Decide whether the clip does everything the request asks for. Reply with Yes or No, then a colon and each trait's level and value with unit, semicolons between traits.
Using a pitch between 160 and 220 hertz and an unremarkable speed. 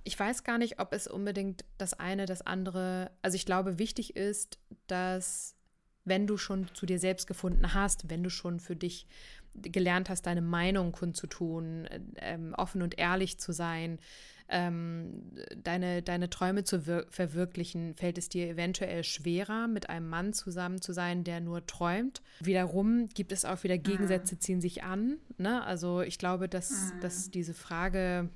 Yes: medium, 185 Hz; average, 165 wpm